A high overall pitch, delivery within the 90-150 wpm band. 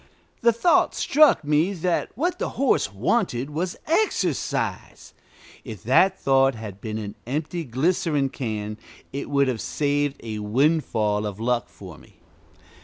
No: medium, 140 Hz; average, 140 wpm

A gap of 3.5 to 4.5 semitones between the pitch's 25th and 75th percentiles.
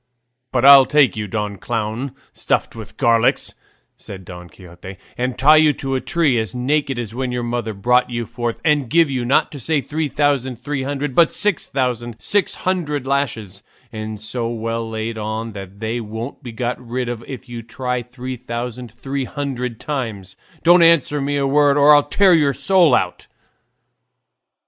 Yes: average, 3.9 semitones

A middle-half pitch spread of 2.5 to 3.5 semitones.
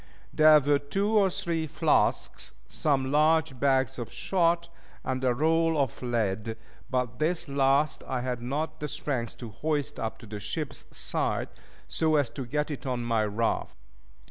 No: average, 4.2 semitones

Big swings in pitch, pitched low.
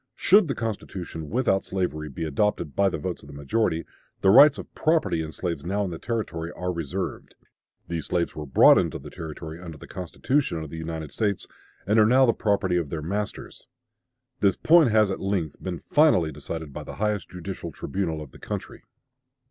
No: average, 4.6 semitones; very low, 90 Hz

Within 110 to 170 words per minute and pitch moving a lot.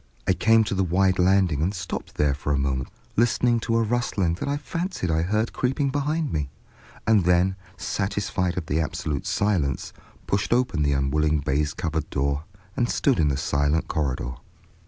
No: average, 180 wpm; wide, 7.0 semitones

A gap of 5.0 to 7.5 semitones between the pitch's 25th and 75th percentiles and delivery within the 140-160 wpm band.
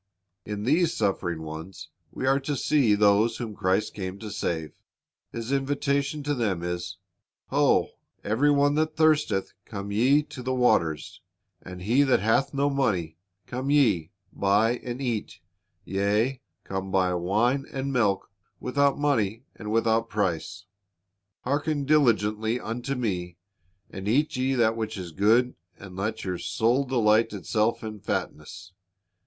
Yes: wide, 5.5 semitones; average, 145 wpm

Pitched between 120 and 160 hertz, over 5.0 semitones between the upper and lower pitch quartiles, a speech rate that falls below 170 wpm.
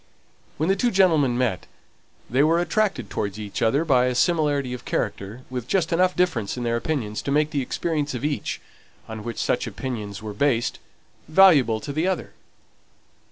No: low, 135 Hz; wide, 5.6 semitones; average, 175 wpm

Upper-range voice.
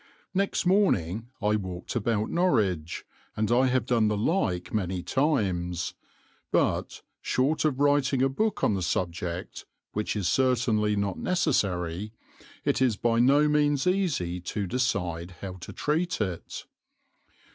No: low, 110 Hz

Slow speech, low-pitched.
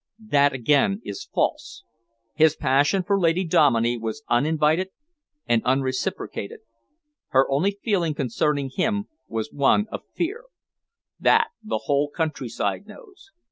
No: slow, 120 wpm; medium, 150 Hz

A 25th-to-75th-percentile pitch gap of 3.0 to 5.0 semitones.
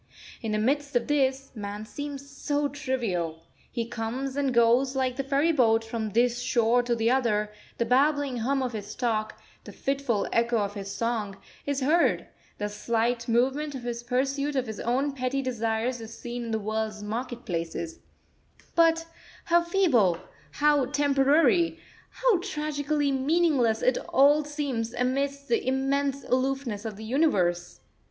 Yes: average, 3.8 semitones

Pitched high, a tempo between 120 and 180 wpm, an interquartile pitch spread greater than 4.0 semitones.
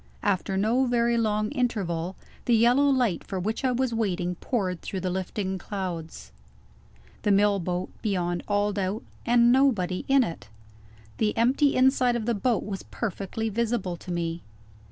Yes: high, 210 Hz; average, 155 wpm; average, 4.5 semitones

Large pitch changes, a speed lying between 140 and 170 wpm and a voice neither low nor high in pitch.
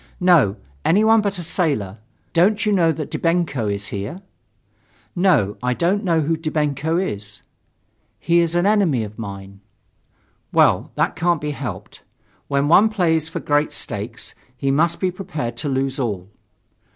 Yes: wide, 6.8 semitones; average, 150 wpm; medium, 155 Hz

